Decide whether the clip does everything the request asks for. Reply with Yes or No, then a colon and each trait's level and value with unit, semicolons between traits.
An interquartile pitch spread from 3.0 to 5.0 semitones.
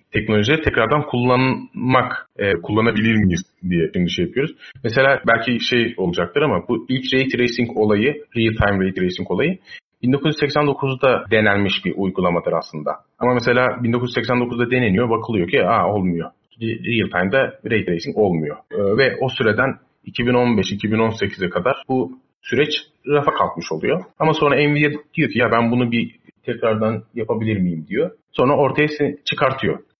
Yes: average, 3.6 semitones